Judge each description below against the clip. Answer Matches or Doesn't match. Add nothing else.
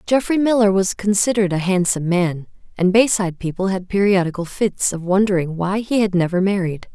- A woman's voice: Matches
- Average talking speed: Matches